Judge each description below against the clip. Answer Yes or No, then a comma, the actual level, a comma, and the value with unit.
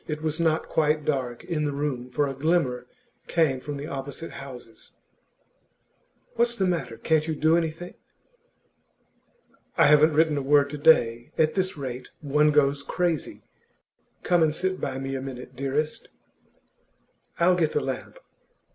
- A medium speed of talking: Yes, average, 155 wpm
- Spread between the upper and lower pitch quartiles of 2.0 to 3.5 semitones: Yes, average, 3.0 semitones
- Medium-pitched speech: Yes, medium, 150 Hz